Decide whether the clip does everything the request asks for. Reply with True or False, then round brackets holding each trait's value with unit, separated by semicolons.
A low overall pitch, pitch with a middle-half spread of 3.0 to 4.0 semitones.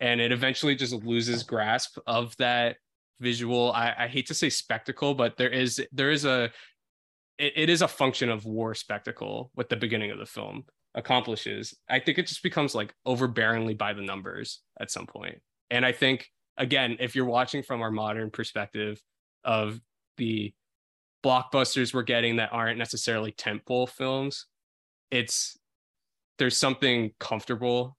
False (120 Hz; 2.4 semitones)